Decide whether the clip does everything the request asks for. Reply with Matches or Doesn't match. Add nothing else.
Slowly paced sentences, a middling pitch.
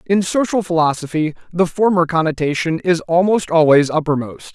Matches